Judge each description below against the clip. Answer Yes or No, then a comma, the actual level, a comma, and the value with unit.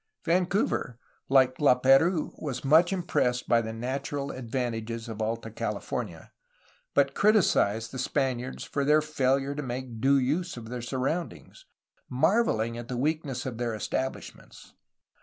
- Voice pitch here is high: No, low, 130 Hz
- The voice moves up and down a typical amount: Yes, average, 4.1 semitones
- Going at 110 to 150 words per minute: Yes, average, 140 wpm